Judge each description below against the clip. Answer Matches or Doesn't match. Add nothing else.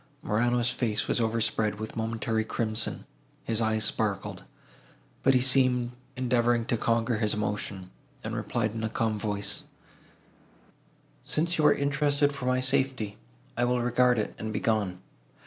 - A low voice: Matches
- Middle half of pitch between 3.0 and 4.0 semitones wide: Doesn't match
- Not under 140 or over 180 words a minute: Matches